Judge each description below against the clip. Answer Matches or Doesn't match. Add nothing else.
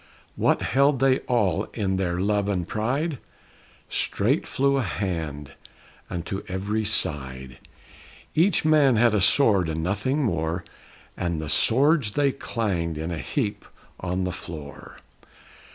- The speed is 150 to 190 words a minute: Doesn't match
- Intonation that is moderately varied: Doesn't match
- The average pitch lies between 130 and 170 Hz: Doesn't match